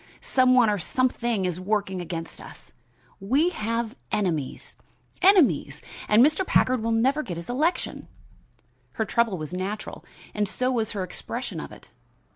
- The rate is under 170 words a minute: Yes, average, 150 wpm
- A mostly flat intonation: No, average, 5.2 semitones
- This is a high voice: Yes, high, 220 Hz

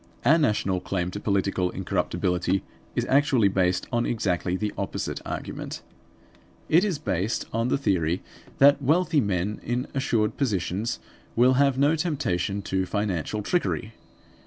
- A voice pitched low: Yes, low, 105 Hz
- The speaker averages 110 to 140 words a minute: Yes, slow, 135 wpm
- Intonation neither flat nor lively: No, wide, 6.5 semitones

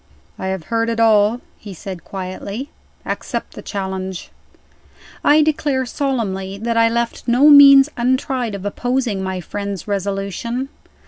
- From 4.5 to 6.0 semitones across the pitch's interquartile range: Yes, average, 4.8 semitones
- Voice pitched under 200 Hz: No, high, 225 Hz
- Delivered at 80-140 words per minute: Yes, slow, 135 wpm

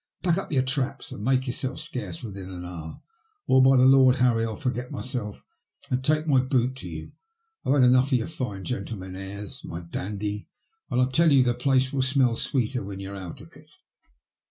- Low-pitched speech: Yes, low, 125 Hz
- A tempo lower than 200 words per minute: No, fast, 205 wpm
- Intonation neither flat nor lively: Yes, average, 4.6 semitones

